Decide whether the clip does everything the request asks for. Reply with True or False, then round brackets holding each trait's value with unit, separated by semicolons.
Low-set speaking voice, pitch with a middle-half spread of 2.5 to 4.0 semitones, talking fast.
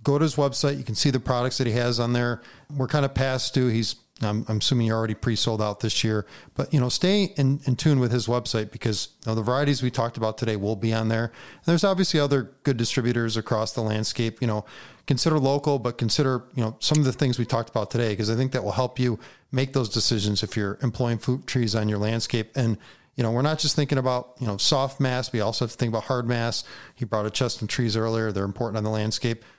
True (120 Hz; 2.9 semitones; 255 wpm)